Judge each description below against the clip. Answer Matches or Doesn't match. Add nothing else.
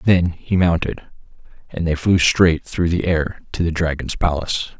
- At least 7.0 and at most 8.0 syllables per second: Doesn't match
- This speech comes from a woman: Doesn't match